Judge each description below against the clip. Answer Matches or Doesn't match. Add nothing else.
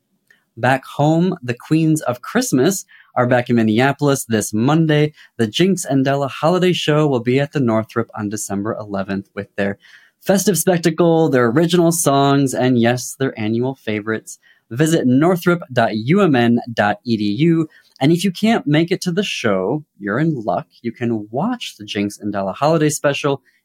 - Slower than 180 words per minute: Matches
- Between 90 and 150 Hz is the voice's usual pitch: Matches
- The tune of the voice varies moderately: Doesn't match